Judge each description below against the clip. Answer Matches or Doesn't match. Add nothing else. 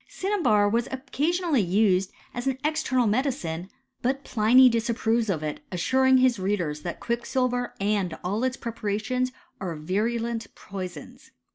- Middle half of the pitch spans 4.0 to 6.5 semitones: Matches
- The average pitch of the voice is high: Matches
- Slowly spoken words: Matches